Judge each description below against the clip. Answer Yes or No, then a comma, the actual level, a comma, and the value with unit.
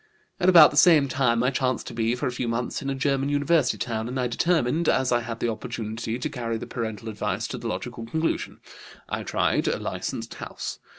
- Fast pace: Yes, fast, 220 wpm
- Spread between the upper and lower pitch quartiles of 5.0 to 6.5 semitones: No, average, 3.3 semitones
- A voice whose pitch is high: No, low, 125 Hz